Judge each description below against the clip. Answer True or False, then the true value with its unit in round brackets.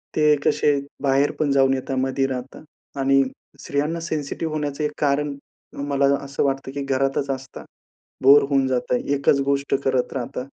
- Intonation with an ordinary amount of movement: False (1.4 semitones)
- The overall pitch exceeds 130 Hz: True (140 Hz)